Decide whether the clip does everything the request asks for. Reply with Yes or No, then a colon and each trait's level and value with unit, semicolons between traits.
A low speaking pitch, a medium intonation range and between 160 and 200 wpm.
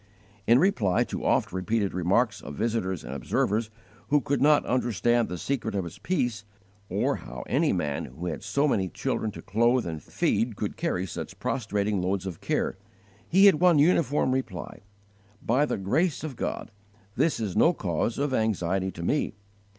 No: low, 110 Hz; wide, 6.6 semitones; average, 175 wpm